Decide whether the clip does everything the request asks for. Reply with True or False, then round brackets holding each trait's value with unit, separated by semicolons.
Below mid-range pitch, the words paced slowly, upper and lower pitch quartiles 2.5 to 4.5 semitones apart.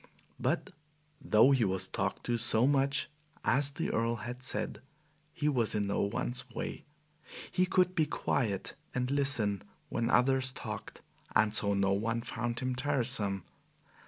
False (120 Hz; 150 wpm; 4.0 semitones)